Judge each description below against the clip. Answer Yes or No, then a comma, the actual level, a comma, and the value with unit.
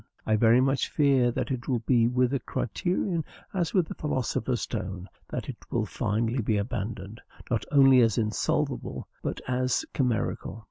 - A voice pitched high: No, low, 120 Hz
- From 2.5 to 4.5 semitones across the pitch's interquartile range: Yes, average, 3.2 semitones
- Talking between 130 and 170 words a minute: Yes, average, 160 wpm